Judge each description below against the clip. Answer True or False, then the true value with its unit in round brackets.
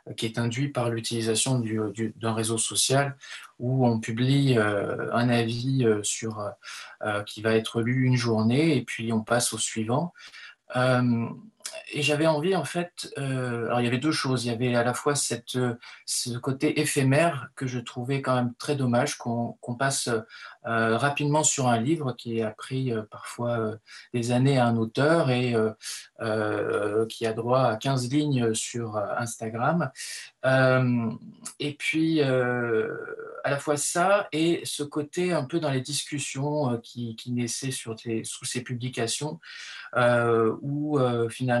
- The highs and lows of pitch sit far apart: False (3.7 semitones)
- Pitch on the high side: False (125 Hz)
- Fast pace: False (170 wpm)